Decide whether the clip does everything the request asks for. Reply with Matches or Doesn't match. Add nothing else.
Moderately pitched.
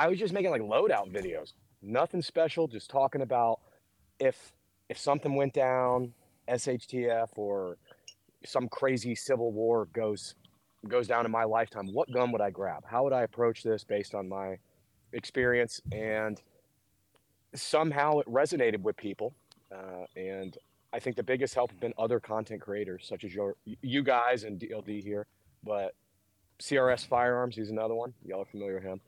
Doesn't match